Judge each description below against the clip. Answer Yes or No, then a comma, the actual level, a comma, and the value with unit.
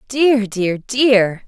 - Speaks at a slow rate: Yes, slow, 120 wpm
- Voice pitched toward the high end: Yes, high, 225 Hz